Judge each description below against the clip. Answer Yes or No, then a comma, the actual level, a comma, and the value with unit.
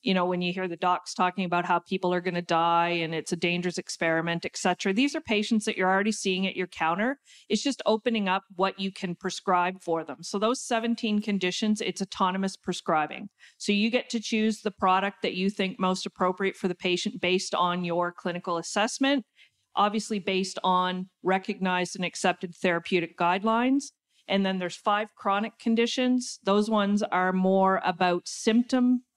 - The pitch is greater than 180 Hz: Yes, high, 190 Hz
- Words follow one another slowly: No, average, 185 wpm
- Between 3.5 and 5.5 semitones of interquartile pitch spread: No, average, 3.0 semitones